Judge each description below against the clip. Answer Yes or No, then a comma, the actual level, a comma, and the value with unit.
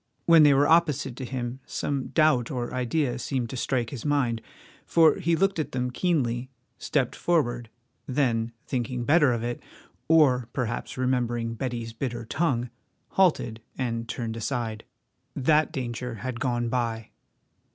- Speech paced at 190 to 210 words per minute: No, average, 145 wpm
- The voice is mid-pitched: No, low, 125 Hz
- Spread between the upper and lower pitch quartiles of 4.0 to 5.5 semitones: No, average, 3.4 semitones